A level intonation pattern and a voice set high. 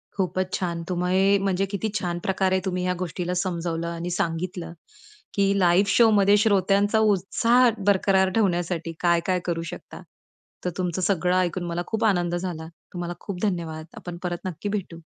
No: narrow, 2.2 semitones; medium, 180 Hz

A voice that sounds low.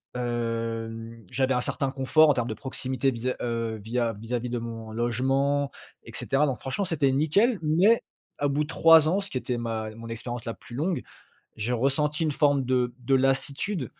Yes: low, 130 Hz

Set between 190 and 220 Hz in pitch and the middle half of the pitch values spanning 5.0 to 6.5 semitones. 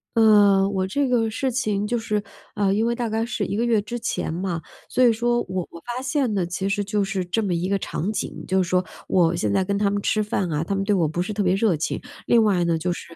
No: high, 200 Hz; average, 3.4 semitones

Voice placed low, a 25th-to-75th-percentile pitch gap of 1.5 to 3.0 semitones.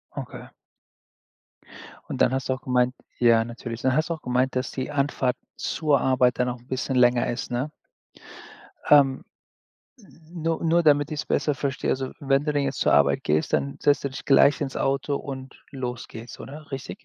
Yes: low, 130 Hz; narrow, 2.5 semitones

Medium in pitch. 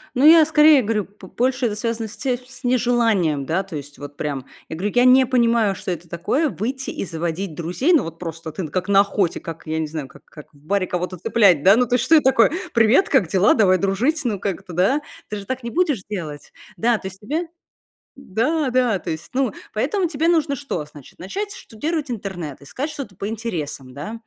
No: high, 210 Hz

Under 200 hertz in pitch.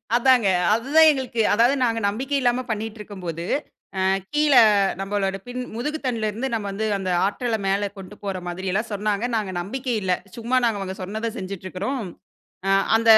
No: high, 220 Hz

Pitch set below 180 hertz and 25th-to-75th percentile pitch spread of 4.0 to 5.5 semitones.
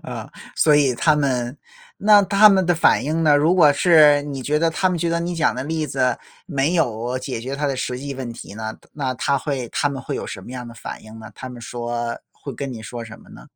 Yes: medium, 140 Hz; average, 4.4 semitones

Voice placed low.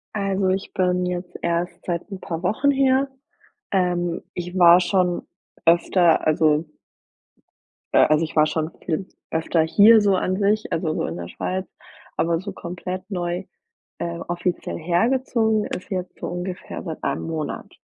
No: medium, 180 Hz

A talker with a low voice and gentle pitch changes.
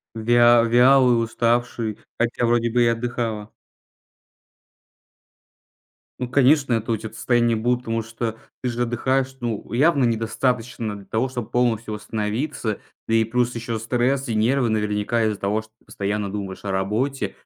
Yes: low, 115 Hz; narrow, 1.9 semitones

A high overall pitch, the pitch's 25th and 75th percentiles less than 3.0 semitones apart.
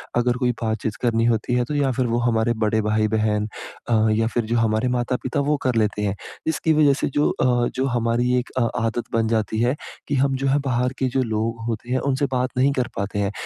No: low, 120 Hz; narrow, 2.6 semitones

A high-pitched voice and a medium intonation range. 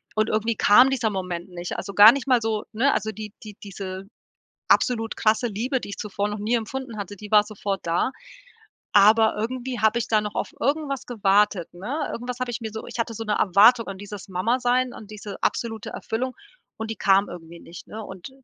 Yes: high, 215 Hz; average, 3.0 semitones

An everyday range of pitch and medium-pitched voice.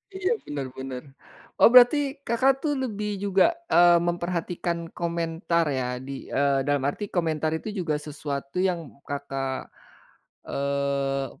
Yes: average, 4.1 semitones; medium, 160 Hz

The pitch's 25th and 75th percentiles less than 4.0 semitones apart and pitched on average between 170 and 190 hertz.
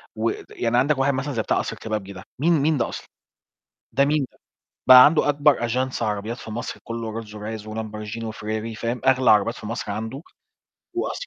No: average, 3.6 semitones; low, 115 Hz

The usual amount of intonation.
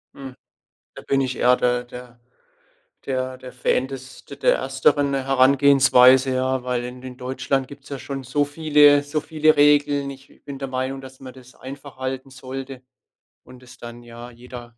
No: narrow, 1.7 semitones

